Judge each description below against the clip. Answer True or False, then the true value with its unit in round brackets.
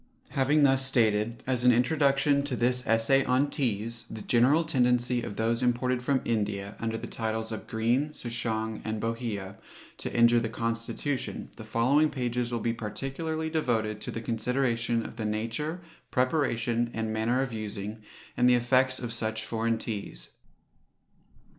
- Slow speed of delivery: False (155 wpm)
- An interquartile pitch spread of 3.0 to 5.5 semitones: False (2.5 semitones)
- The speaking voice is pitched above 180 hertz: False (120 Hz)